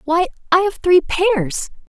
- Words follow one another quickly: No, average, 150 wpm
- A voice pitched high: Yes, very high, 335 Hz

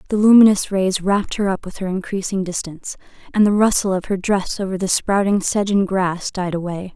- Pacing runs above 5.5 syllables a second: Yes, 5.7 syllables/s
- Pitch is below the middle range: No, high, 190 Hz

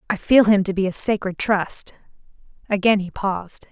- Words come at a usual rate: Yes, average, 180 wpm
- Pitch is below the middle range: No, high, 200 Hz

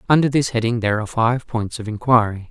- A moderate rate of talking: No, fast, 215 wpm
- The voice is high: No, low, 115 Hz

